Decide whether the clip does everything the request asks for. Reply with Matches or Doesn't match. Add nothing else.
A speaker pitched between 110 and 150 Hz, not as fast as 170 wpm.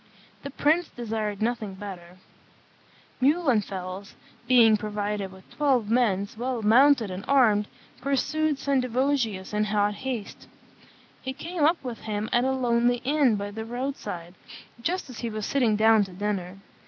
Doesn't match